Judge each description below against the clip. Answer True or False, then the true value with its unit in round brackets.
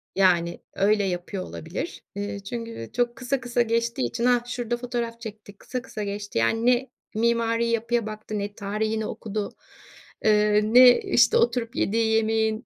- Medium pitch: False (225 Hz)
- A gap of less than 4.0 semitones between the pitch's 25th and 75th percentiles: True (2.7 semitones)